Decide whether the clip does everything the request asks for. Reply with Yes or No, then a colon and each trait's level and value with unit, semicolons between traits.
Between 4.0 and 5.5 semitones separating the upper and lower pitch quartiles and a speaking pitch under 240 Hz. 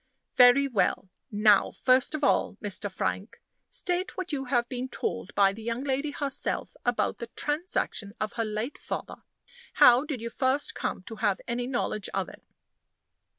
No: average, 4.7 semitones; high, 245 Hz